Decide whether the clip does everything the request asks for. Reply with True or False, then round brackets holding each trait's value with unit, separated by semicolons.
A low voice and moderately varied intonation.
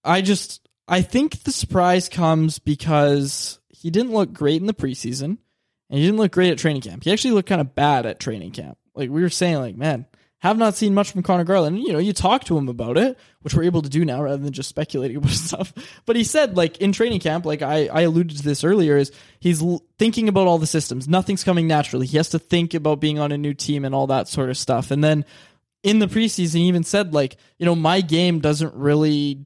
False (165 Hz; 4.6 semitones)